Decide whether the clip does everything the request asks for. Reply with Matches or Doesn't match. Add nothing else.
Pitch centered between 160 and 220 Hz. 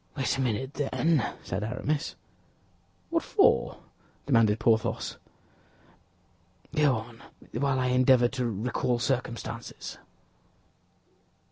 Doesn't match